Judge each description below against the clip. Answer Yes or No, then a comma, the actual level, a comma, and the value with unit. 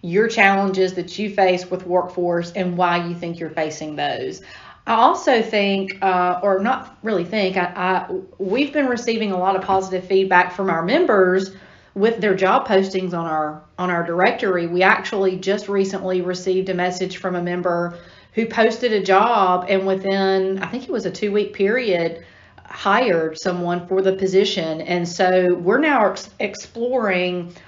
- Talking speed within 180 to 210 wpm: No, average, 170 wpm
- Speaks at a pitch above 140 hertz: Yes, high, 190 Hz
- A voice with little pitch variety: Yes, narrow, 1.9 semitones